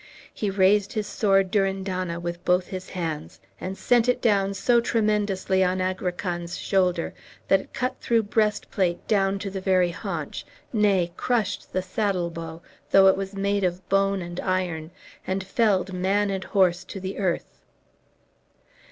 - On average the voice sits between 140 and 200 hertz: Yes, high, 190 Hz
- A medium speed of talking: Yes, average, 155 wpm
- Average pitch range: No, narrow, 1.9 semitones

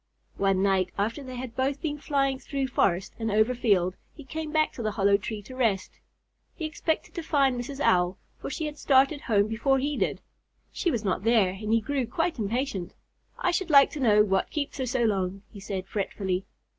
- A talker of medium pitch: No, high, 235 Hz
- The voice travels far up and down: Yes, wide, 5.8 semitones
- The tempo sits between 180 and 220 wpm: Yes, fast, 205 wpm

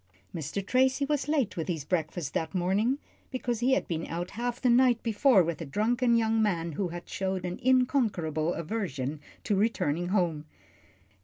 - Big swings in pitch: Yes, wide, 6.5 semitones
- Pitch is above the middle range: Yes, high, 195 Hz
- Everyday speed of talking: Yes, average, 170 wpm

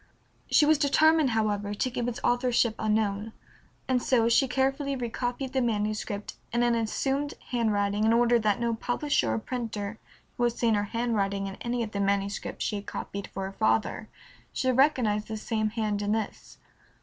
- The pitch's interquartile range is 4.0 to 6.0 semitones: No, average, 3.1 semitones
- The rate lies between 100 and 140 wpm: No, average, 175 wpm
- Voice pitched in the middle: No, high, 225 Hz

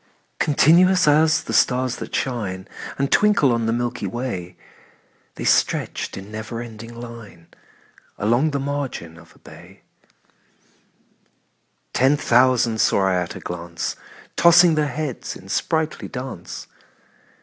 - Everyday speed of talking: No, slow, 125 wpm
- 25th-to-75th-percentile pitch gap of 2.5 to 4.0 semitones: No, average, 5.1 semitones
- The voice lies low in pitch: Yes, low, 120 Hz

